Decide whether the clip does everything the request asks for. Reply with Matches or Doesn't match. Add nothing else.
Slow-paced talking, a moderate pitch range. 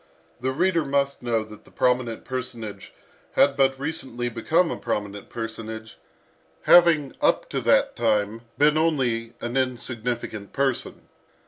Matches